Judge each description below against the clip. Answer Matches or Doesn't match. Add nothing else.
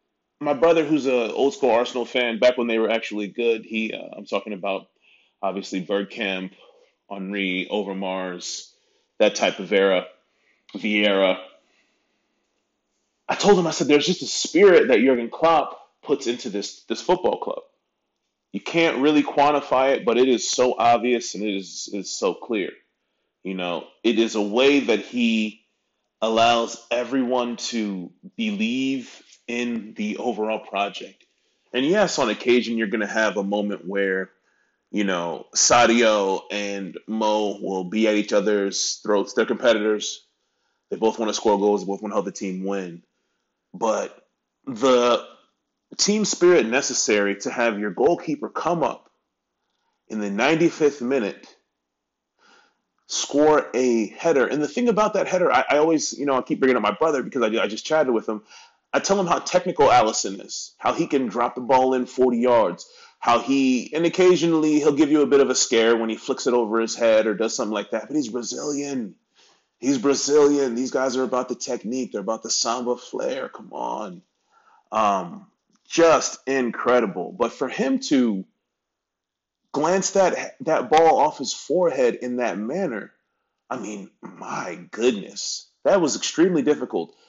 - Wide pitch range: Matches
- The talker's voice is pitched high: Doesn't match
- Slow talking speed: Doesn't match